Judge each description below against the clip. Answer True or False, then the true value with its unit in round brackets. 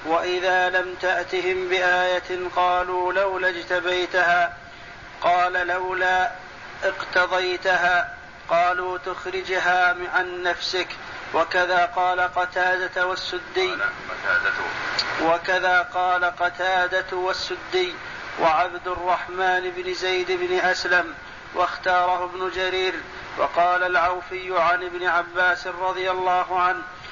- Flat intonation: True (0.5 semitones)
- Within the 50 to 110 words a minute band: True (85 wpm)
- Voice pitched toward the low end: False (180 Hz)